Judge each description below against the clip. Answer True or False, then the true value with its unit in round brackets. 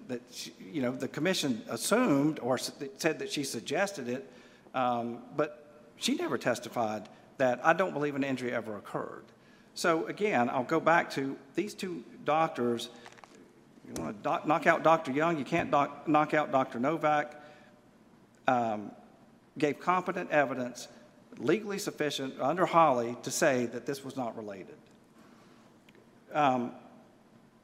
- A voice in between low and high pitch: True (145 Hz)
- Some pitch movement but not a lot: True (4.7 semitones)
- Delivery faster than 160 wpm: False (135 wpm)